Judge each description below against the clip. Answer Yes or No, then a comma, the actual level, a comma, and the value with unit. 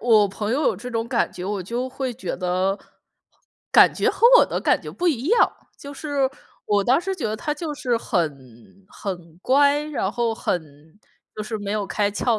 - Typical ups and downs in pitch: No, wide, 5.7 semitones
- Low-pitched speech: No, high, 225 Hz